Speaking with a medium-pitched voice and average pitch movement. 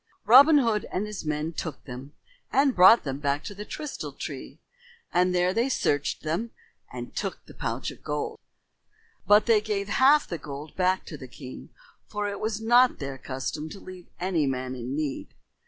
No: medium, 180 Hz; wide, 6.8 semitones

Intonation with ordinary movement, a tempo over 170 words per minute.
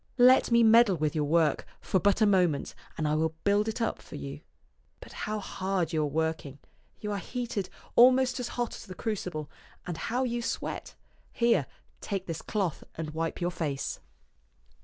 No: wide, 6.2 semitones; average, 180 wpm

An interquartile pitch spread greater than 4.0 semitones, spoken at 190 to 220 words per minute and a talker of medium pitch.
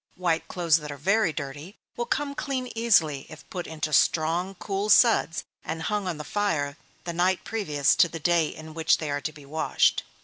Yes: average, 4.4 semitones; average, 200 wpm; medium, 165 Hz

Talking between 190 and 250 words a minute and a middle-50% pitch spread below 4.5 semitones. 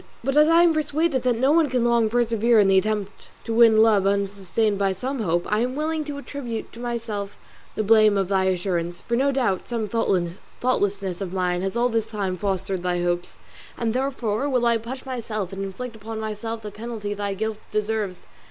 Yes: average, 200 wpm; average, 3.6 semitones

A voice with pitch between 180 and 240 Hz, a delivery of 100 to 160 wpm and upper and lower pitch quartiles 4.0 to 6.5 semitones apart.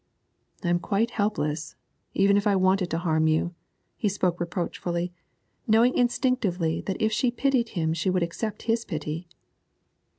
Yes: medium, 185 Hz; average, 155 wpm; average, 4.3 semitones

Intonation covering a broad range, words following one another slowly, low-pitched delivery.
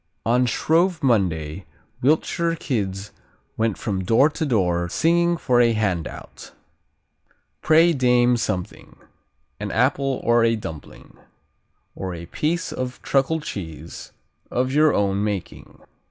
Yes: wide, 6.8 semitones; slow, 120 wpm; low, 120 Hz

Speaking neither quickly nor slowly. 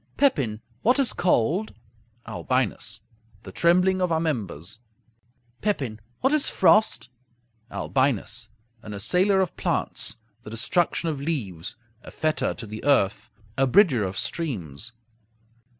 No: slow, 120 wpm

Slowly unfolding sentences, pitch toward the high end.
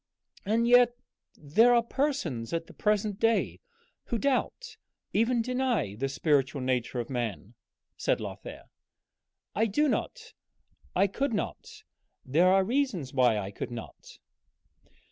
Yes: slow, 130 wpm; high, 205 Hz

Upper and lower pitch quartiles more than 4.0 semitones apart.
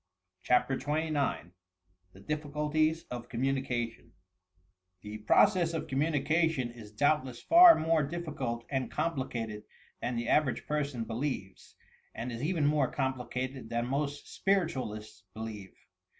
Yes: average, 4.5 semitones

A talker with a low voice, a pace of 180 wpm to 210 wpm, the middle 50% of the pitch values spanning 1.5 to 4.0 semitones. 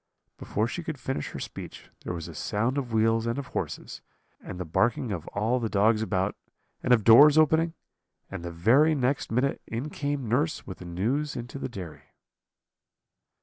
No: low, 115 Hz; average, 185 wpm; average, 5.1 semitones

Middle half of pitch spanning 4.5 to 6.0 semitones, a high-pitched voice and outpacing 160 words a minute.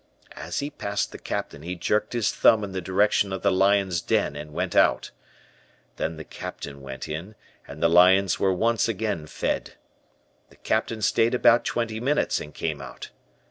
No: average, 4.9 semitones; very low, 95 Hz; average, 180 wpm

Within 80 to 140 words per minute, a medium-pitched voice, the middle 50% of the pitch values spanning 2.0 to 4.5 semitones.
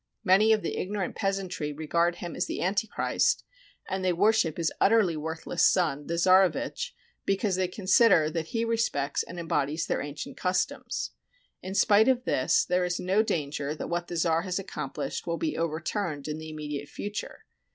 No: average, 170 wpm; medium, 180 Hz; average, 4.0 semitones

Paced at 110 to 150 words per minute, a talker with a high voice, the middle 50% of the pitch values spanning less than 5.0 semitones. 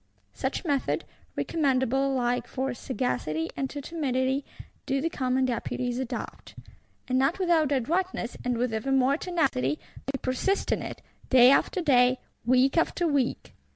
Yes: average, 145 wpm; very high, 265 Hz; narrow, 2.4 semitones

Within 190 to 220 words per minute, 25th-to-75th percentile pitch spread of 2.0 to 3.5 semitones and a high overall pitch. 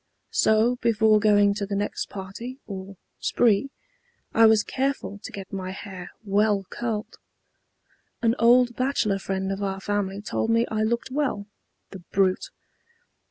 No: average, 145 wpm; average, 2.8 semitones; high, 210 Hz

